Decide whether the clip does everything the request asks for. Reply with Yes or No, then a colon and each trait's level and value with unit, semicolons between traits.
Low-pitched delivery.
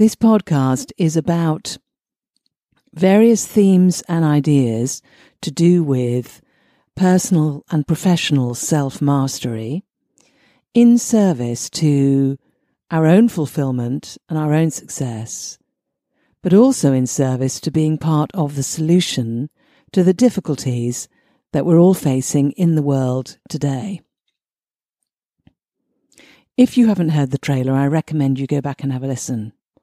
No: medium, 155 Hz